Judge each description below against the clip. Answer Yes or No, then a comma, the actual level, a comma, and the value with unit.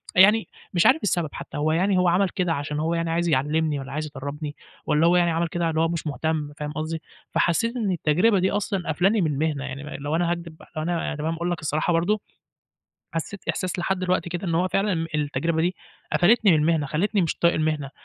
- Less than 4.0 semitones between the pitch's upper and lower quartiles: Yes, average, 2.8 semitones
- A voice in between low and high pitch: Yes, medium, 165 Hz